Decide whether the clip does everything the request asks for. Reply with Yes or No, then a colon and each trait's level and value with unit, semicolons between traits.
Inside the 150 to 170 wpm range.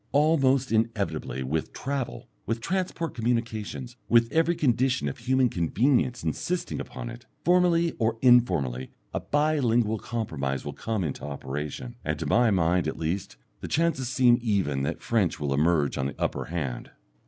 Yes: average, 155 wpm